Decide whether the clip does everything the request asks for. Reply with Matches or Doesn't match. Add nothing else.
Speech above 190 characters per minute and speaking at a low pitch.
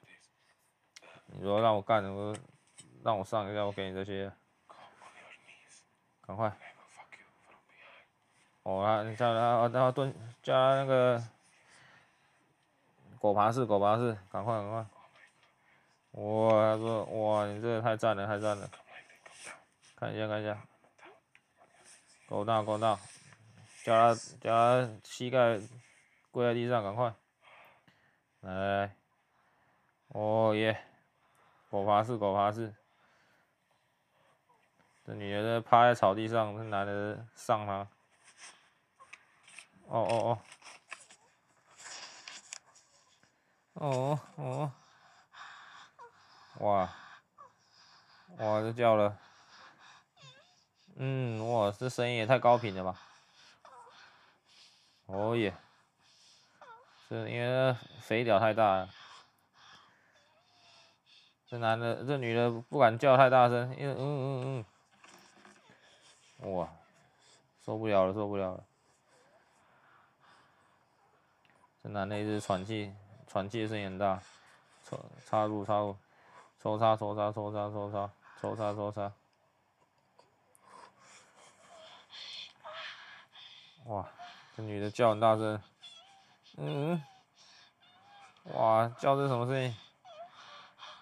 Doesn't match